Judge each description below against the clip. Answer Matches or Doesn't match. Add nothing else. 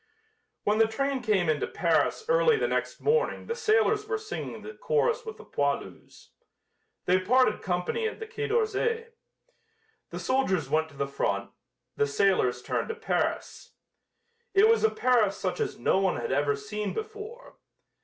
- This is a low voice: Doesn't match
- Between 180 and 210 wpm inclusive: Doesn't match